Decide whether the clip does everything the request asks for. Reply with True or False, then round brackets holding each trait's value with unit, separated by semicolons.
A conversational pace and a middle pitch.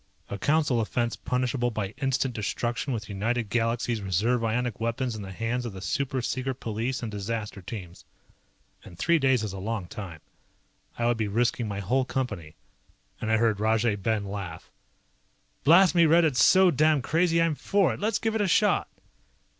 False (180 wpm; 115 Hz)